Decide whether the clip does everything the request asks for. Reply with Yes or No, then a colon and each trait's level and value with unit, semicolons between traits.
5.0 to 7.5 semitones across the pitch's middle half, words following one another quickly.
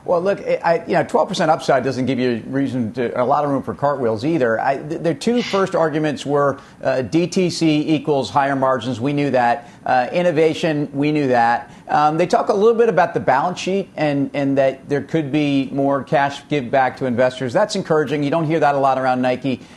No: average, 3.5 semitones; fast, 215 wpm